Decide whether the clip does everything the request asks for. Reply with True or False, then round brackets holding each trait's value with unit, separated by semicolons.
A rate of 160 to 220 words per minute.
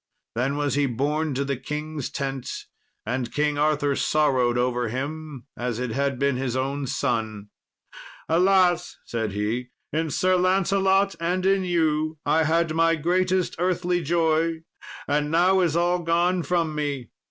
False (150 wpm)